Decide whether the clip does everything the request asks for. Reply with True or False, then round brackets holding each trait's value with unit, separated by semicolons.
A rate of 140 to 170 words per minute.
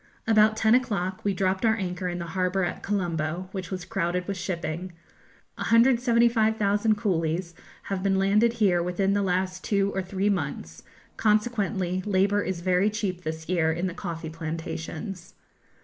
True (155 wpm)